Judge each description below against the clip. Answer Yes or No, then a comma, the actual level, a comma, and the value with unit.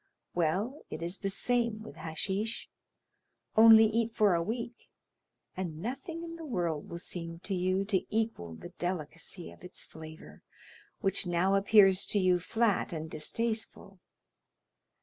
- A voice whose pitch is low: No, high, 195 Hz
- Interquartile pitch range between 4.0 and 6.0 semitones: Yes, average, 4.5 semitones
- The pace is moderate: Yes, average, 145 wpm